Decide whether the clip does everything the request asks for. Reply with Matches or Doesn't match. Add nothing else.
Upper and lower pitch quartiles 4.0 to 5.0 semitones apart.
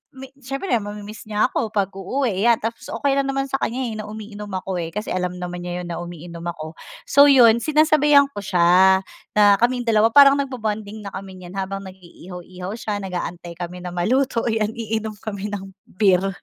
Matches